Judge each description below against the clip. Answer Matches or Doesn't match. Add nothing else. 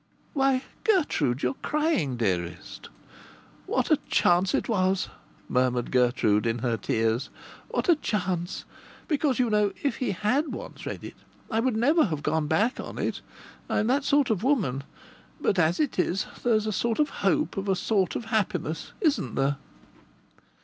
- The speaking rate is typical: Matches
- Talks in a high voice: Matches